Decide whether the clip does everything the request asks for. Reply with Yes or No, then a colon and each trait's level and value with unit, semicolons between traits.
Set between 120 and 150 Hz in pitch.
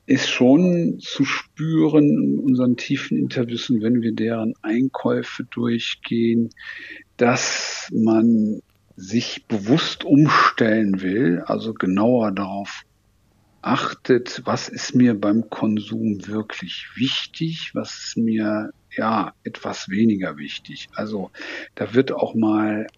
No: low, 110 Hz